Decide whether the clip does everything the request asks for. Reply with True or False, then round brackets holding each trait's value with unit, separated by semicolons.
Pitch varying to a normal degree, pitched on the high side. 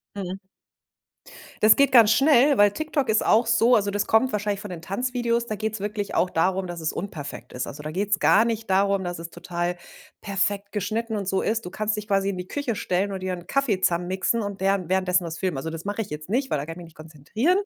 True (3.7 semitones; 200 Hz)